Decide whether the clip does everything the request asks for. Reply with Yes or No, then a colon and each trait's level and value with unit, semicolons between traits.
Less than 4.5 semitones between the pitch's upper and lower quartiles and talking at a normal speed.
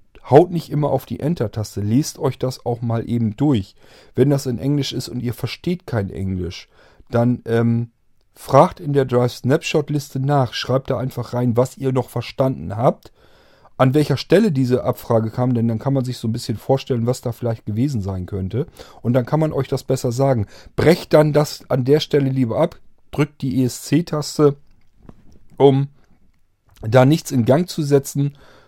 Yes: average, 3.2 semitones; average, 180 wpm